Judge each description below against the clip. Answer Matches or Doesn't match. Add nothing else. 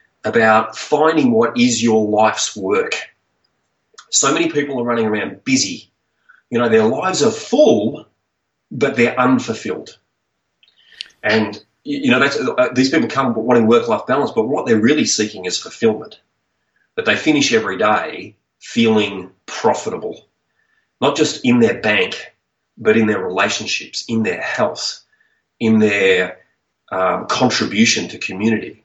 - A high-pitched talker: Doesn't match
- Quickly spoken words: Doesn't match